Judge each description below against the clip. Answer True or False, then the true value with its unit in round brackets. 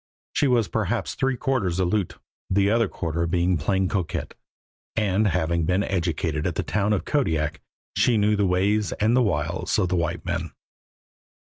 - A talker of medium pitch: False (95 Hz)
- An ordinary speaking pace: True (165 wpm)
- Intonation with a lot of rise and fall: False (3.9 semitones)